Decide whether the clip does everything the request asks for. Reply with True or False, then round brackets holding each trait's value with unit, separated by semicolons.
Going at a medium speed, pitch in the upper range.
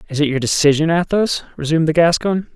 False (190 wpm; 160 Hz)